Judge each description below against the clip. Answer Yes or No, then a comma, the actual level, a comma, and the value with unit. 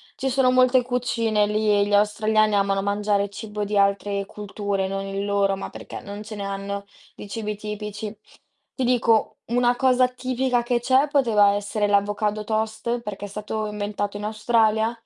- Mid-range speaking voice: No, high, 210 Hz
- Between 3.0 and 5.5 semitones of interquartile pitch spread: No, narrow, 2.5 semitones